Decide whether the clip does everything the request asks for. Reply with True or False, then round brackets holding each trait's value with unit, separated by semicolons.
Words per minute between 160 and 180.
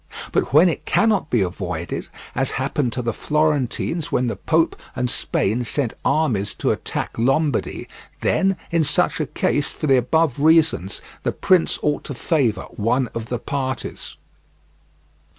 False (150 wpm)